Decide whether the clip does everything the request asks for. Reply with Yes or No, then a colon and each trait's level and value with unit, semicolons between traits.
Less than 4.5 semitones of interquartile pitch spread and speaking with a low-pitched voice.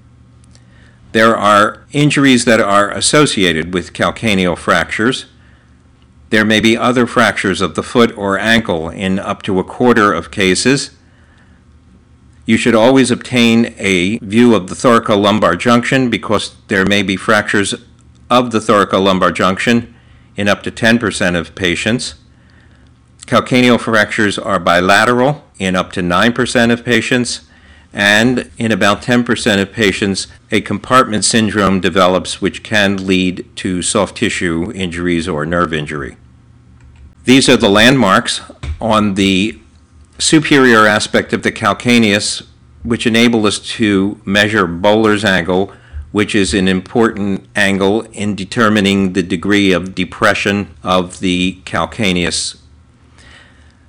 Yes: average, 4.1 semitones; low, 100 Hz